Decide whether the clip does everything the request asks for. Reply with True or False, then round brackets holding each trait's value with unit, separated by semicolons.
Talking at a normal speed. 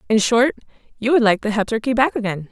False (215 wpm)